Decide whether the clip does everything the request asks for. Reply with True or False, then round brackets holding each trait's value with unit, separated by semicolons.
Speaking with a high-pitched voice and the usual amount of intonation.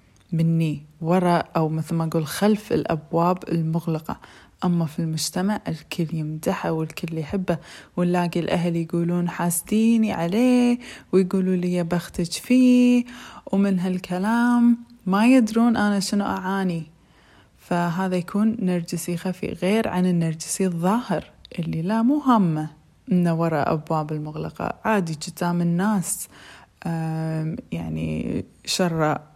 False (175 Hz; 3.7 semitones)